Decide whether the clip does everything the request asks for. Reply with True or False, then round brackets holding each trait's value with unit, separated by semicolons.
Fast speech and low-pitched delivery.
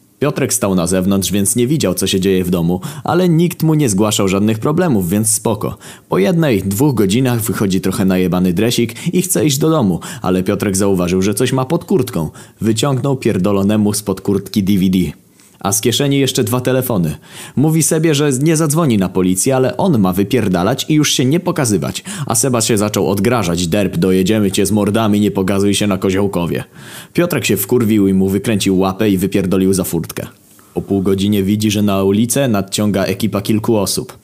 True (190 wpm; 105 Hz)